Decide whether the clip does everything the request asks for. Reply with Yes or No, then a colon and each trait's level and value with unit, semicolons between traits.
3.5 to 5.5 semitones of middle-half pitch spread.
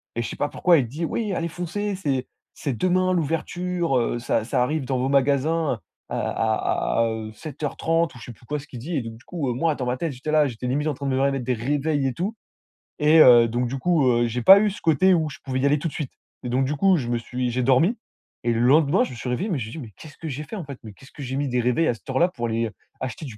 Yes: average, 4.7 semitones